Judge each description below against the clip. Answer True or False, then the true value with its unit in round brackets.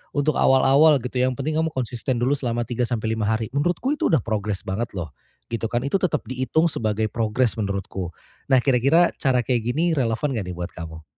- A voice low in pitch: True (120 Hz)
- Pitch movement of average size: True (4.2 semitones)